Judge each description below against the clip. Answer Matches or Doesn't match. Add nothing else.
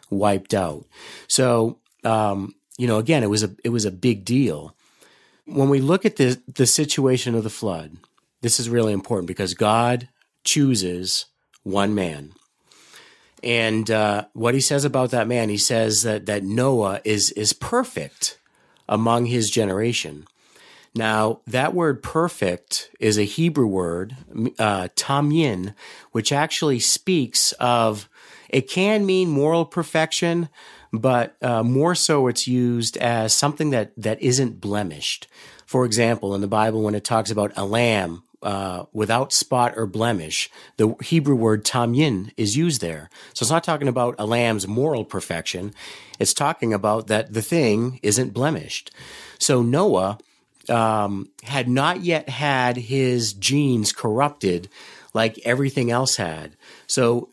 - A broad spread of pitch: Doesn't match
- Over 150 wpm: Doesn't match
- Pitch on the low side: Matches